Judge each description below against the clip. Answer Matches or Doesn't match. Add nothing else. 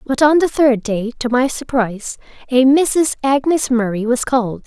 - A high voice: Matches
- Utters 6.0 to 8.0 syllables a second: Doesn't match